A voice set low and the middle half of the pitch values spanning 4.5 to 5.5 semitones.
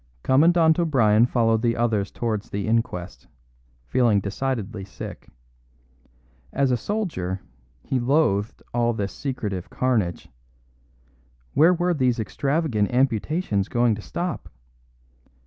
Yes: low, 120 Hz; average, 5.0 semitones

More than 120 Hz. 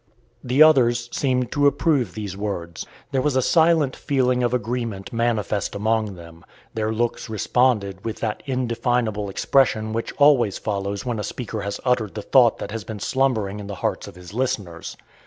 No: low, 115 Hz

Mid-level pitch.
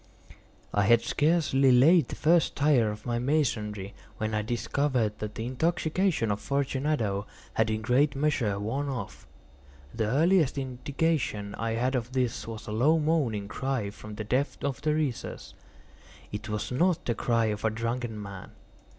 No: low, 125 Hz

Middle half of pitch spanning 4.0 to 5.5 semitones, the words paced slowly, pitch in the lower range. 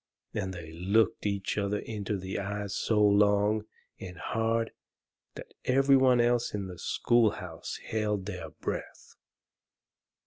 No: average, 2.8 semitones; slow, 130 wpm; low, 105 Hz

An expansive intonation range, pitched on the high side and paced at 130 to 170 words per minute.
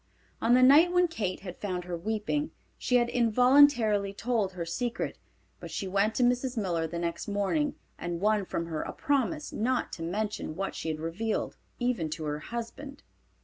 No: wide, 5.7 semitones; high, 215 Hz; average, 185 wpm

